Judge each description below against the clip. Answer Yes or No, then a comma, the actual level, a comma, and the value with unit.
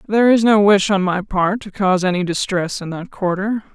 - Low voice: No, high, 195 Hz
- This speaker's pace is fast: Yes, fast, 225 wpm